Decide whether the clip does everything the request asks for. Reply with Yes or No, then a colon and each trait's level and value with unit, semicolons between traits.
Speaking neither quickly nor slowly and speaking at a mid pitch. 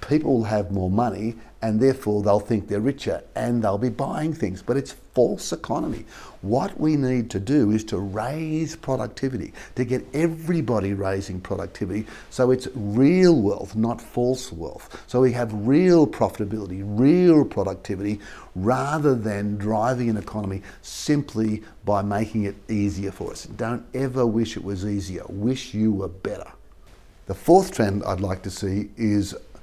No: average, 160 wpm; low, 110 Hz